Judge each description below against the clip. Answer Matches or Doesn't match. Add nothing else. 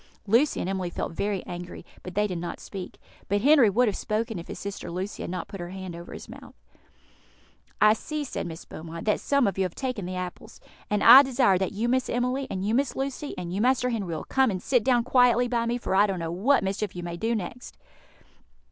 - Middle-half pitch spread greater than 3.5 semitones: Matches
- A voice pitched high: Matches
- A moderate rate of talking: Doesn't match